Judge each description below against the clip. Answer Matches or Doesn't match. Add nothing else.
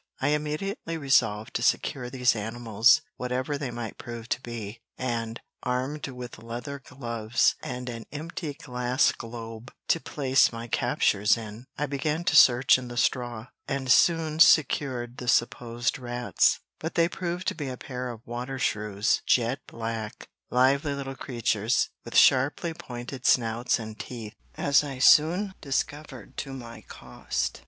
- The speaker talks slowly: Doesn't match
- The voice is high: Doesn't match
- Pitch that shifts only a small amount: Doesn't match